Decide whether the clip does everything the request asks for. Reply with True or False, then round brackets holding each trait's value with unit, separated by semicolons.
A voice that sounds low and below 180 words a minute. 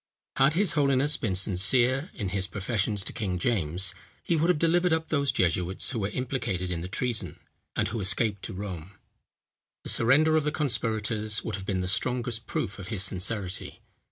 False (110 Hz; 185 wpm)